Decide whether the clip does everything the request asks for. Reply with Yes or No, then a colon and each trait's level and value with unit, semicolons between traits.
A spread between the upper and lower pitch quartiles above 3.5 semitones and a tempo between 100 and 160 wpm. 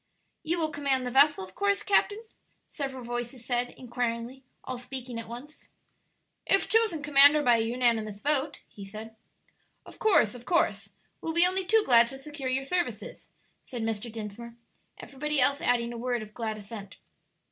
No: average, 4.3 semitones; average, 170 wpm